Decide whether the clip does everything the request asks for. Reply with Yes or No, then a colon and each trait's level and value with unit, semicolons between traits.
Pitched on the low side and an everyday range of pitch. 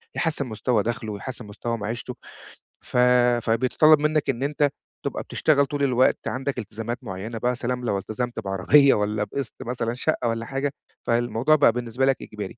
Yes: low, 120 Hz; average, 3.5 semitones